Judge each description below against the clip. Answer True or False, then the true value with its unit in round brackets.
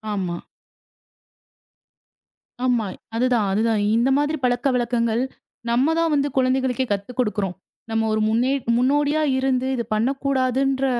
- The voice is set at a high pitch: True (250 Hz)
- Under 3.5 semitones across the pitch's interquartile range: True (2.9 semitones)